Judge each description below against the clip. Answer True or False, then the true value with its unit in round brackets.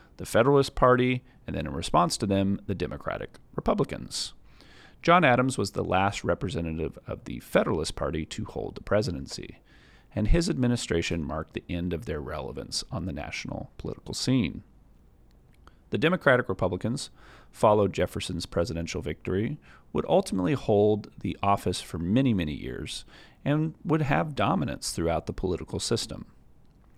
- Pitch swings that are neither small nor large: False (6.6 semitones)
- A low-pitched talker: True (100 Hz)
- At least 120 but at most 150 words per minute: True (140 wpm)